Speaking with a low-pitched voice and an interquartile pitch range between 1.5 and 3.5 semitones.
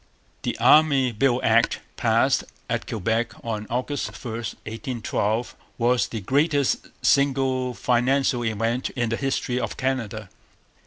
Yes: low, 125 Hz; average, 2.9 semitones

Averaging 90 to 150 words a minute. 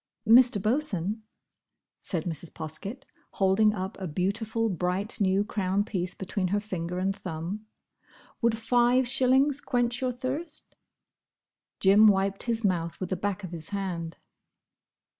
Yes: slow, 135 wpm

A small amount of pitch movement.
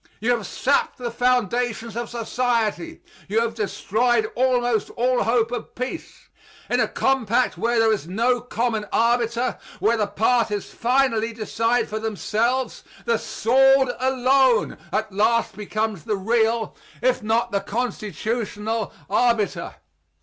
Yes: narrow, 2.2 semitones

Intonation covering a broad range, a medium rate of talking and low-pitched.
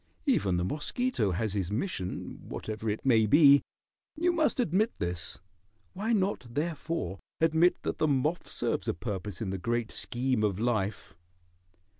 Yes: wide, 8.7 semitones; average, 150 wpm; low, 120 Hz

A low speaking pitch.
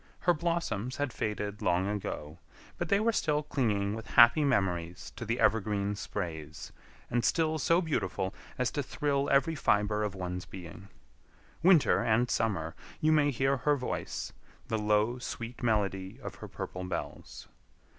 Yes: low, 110 Hz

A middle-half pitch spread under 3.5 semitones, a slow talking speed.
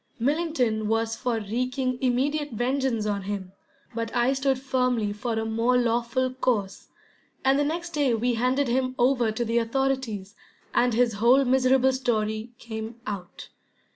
No: average, 2.8 semitones; average, 150 wpm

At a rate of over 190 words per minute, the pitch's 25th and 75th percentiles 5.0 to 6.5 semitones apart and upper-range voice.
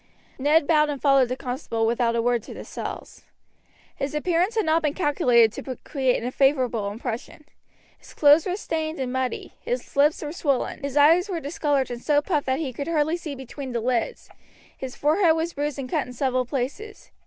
No: average, 200 wpm; average, 3.8 semitones; very high, 280 Hz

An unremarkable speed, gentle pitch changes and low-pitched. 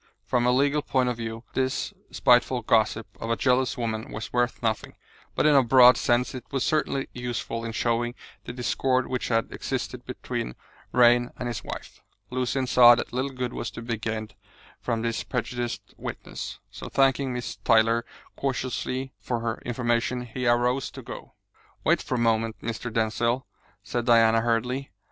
Yes: average, 170 wpm; narrow, 1.8 semitones; low, 120 Hz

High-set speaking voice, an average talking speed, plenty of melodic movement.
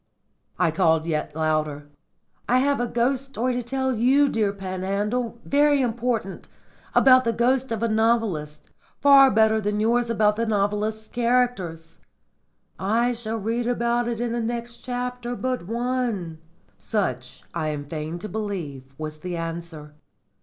Yes: high, 225 Hz; average, 145 wpm; wide, 5.8 semitones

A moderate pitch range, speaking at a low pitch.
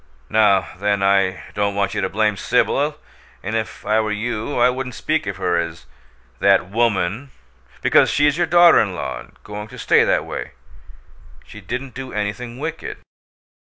Yes: average, 4.0 semitones; low, 105 Hz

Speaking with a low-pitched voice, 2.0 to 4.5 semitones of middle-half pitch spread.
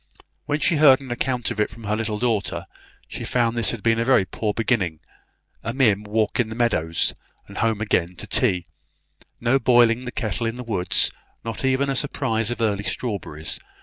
Yes: low, 115 Hz; average, 2.9 semitones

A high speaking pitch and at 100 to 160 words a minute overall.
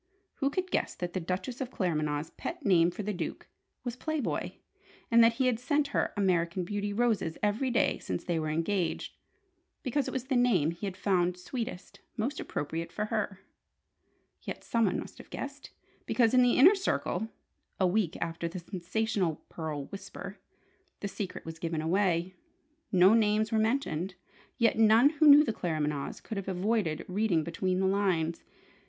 No: high, 200 Hz; average, 170 wpm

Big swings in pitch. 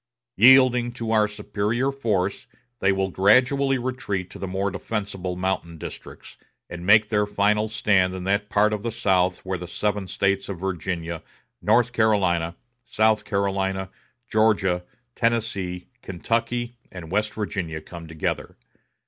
No: average, 2.9 semitones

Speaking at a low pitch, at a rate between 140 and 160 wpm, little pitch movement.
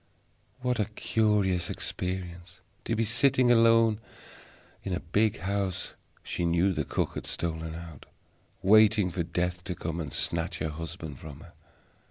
No: very low, 90 Hz; average, 155 wpm; average, 4.1 semitones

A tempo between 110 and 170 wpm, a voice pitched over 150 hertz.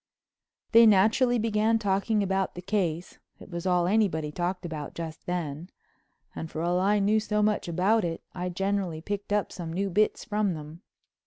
Yes: average, 165 wpm; high, 190 Hz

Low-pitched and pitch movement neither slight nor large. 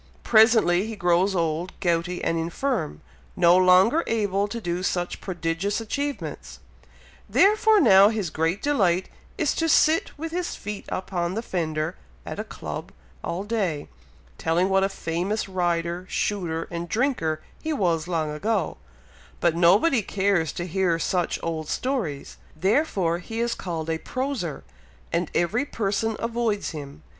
No: medium, 185 Hz; average, 4.8 semitones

